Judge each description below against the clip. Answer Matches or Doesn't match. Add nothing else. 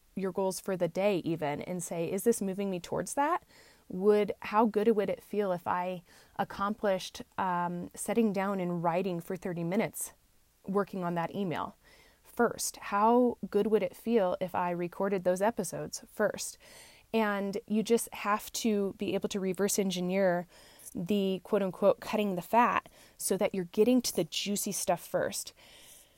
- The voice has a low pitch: Doesn't match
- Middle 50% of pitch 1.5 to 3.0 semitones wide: Matches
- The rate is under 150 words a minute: Doesn't match